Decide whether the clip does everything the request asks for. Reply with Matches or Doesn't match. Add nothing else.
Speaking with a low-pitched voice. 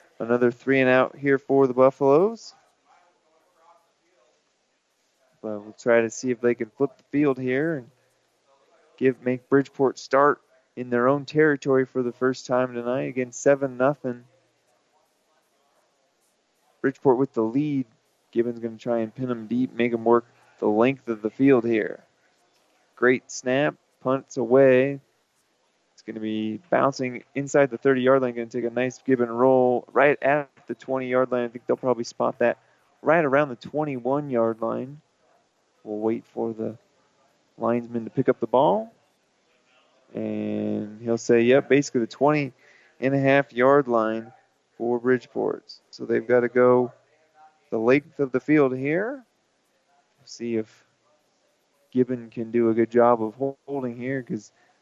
Matches